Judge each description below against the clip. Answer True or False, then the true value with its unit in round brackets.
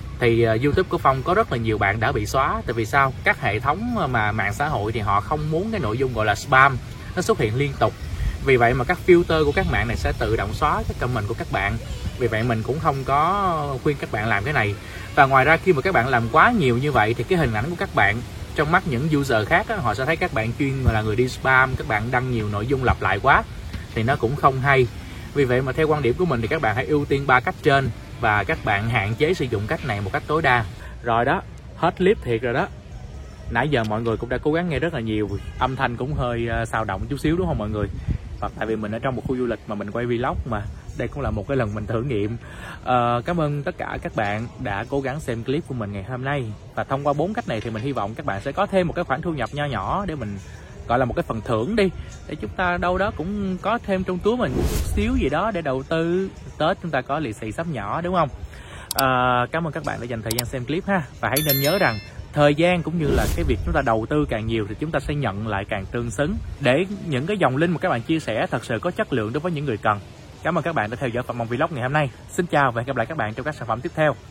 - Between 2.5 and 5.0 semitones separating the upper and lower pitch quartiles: False (5.6 semitones)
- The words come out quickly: True (290 wpm)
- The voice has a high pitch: False (130 Hz)